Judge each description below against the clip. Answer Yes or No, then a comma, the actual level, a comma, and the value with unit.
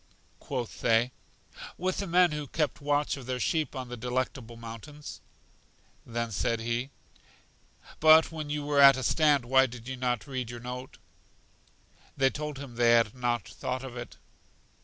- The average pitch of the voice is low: Yes, low, 130 Hz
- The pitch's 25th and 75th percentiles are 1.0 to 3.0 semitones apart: No, average, 3.5 semitones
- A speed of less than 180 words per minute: Yes, average, 165 wpm